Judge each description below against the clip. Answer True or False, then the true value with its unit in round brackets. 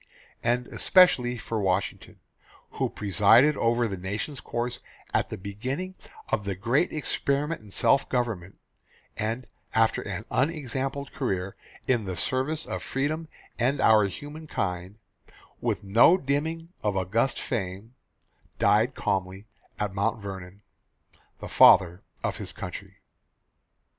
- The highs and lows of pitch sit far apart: True (5.7 semitones)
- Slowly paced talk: True (125 wpm)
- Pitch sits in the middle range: False (115 Hz)